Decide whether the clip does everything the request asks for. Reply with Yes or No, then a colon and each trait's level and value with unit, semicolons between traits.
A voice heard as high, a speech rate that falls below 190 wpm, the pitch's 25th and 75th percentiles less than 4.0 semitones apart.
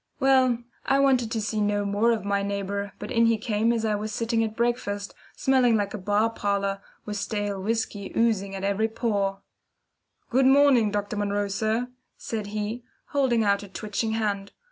Yes: high, 215 Hz; average, 180 wpm; narrow, 2.4 semitones